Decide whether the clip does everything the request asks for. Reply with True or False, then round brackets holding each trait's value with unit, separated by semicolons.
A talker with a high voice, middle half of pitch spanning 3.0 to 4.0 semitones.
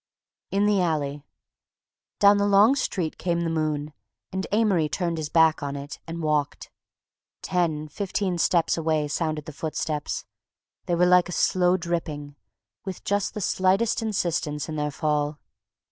False (165 Hz; 3.6 semitones)